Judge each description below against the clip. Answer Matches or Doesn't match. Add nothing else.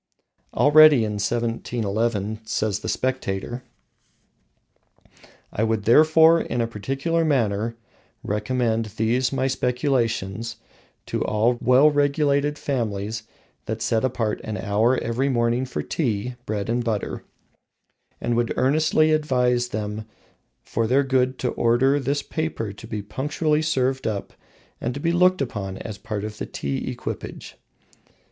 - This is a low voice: Matches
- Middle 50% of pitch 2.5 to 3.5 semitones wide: Doesn't match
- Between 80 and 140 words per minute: Matches